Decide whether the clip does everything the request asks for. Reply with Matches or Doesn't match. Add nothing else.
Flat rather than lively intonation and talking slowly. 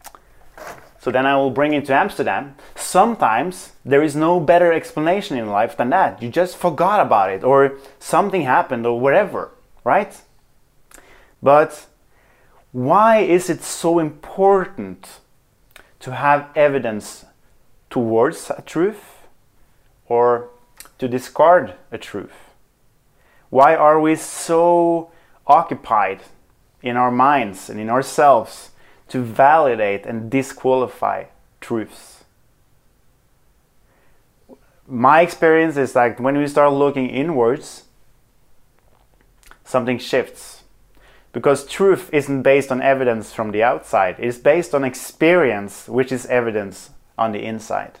Doesn't match